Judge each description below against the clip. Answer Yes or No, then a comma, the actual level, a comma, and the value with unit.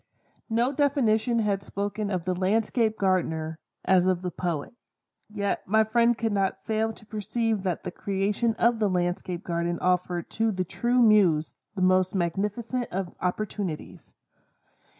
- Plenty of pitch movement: No, average, 3.5 semitones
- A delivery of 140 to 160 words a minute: Yes, average, 150 wpm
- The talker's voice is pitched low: No, high, 200 Hz